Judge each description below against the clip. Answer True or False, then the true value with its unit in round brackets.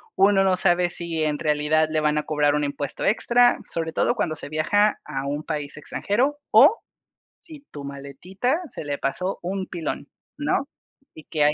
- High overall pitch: False (160 Hz)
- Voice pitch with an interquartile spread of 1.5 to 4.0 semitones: False (4.7 semitones)